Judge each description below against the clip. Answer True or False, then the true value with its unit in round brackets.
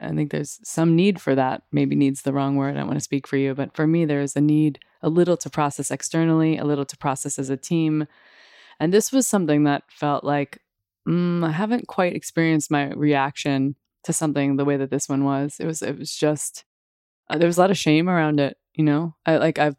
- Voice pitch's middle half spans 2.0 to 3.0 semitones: True (2.7 semitones)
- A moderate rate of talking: False (230 wpm)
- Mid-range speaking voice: True (150 Hz)